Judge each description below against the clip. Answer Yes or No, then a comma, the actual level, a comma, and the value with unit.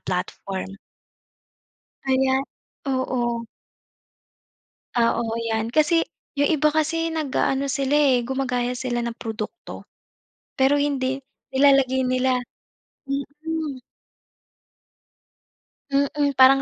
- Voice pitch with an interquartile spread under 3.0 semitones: Yes, narrow, 2.5 semitones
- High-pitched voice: Yes, very high, 265 Hz